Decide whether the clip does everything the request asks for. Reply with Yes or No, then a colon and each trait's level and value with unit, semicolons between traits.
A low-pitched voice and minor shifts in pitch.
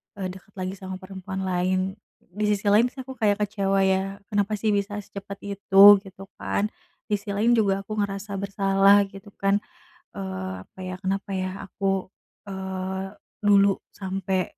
No: high, 195 Hz; narrow, 1.2 semitones